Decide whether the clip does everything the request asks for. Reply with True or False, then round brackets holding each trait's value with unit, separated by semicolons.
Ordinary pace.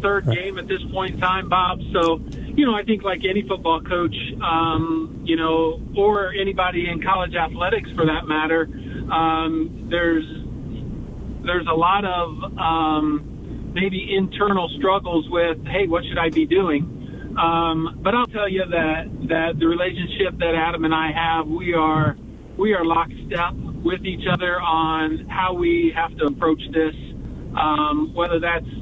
True (160 wpm)